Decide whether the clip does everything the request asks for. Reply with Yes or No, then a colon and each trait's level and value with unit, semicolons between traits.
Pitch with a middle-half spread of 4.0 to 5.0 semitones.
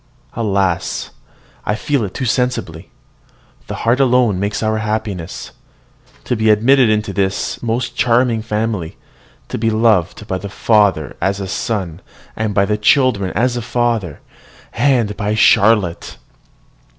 No: average, 3.0 semitones